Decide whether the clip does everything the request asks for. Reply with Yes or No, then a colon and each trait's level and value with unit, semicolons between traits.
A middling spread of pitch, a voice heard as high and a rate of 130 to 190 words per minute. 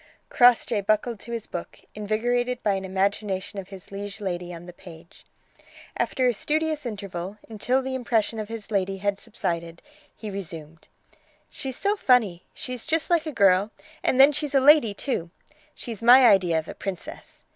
Yes: average, 4.7 semitones; high, 210 Hz; average, 170 wpm